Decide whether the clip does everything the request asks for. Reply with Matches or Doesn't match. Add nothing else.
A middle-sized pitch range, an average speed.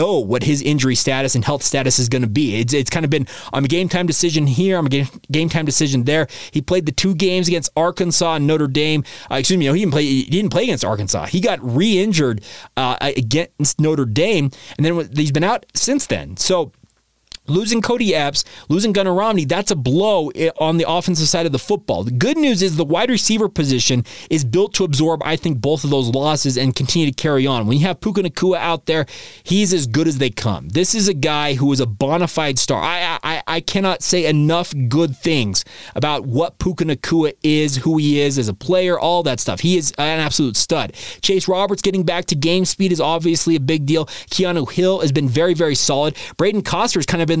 Doesn't match